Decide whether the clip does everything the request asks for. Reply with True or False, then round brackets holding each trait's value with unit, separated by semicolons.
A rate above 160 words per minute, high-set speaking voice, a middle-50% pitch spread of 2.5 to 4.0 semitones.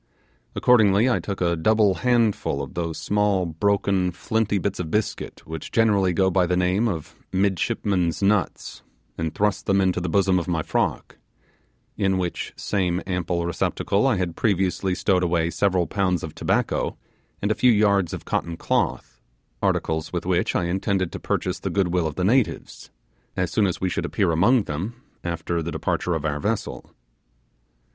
False (170 wpm; 95 Hz; 2.9 semitones)